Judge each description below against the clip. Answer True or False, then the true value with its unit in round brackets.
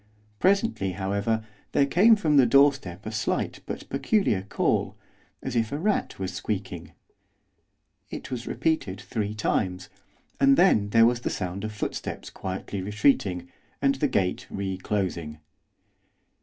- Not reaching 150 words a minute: True (140 wpm)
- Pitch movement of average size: False (6.3 semitones)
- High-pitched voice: False (105 Hz)